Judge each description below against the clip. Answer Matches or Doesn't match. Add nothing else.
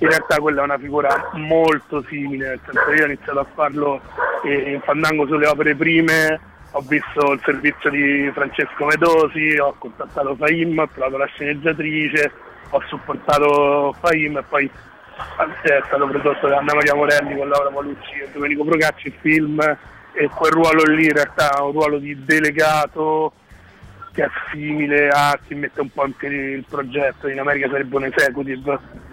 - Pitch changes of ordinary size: Doesn't match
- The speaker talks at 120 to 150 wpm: Doesn't match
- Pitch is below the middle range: Doesn't match